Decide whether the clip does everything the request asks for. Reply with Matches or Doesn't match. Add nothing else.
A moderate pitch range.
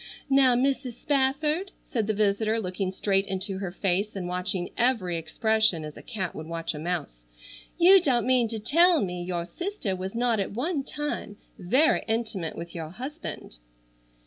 Doesn't match